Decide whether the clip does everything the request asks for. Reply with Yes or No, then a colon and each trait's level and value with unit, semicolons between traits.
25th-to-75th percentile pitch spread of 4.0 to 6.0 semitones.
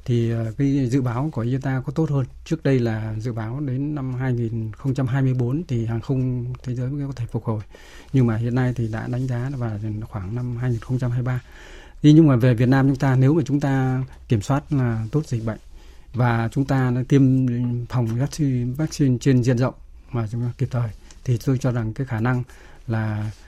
No: average, 2.7 semitones